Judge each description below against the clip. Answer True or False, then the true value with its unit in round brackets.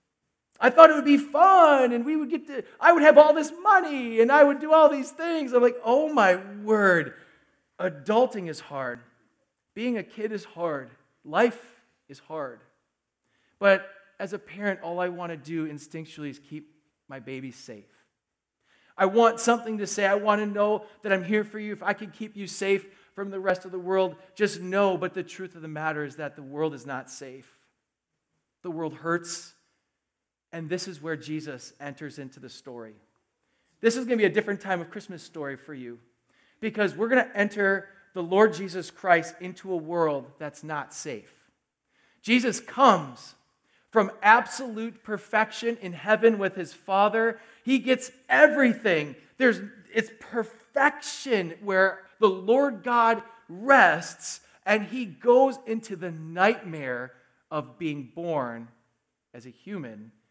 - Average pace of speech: True (170 wpm)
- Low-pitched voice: False (195 Hz)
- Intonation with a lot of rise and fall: True (6.3 semitones)